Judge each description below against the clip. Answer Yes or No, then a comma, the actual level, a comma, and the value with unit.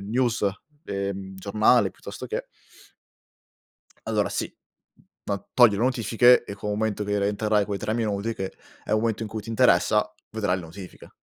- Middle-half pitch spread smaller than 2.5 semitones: Yes, narrow, 2.1 semitones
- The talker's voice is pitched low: Yes, low, 105 Hz